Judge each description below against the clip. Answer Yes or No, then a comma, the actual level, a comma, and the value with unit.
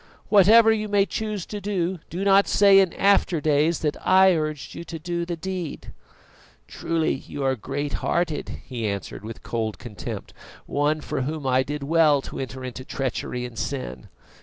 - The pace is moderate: Yes, average, 170 wpm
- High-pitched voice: No, medium, 155 Hz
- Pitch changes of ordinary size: No, wide, 6.2 semitones